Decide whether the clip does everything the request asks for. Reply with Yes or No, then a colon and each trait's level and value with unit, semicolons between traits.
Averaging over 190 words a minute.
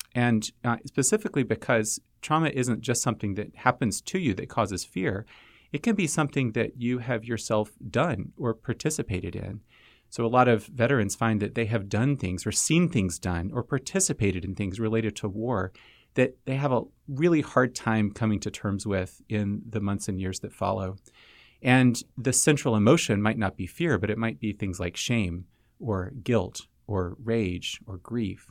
No: average, 185 wpm